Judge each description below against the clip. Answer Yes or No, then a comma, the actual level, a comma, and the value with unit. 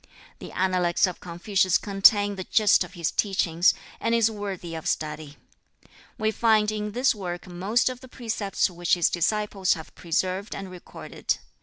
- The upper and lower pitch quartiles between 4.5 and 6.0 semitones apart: No, average, 3.4 semitones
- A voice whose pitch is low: No, high, 195 Hz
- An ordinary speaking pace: Yes, average, 160 wpm